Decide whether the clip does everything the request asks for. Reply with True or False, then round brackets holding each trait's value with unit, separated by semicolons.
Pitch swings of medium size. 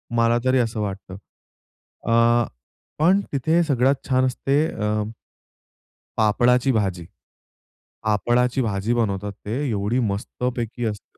True (3.6 semitones)